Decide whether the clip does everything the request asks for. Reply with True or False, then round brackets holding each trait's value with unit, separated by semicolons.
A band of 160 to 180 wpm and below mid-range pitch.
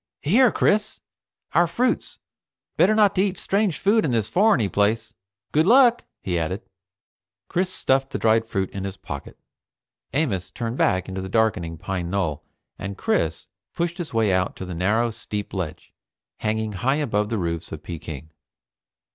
True (165 wpm; 110 Hz)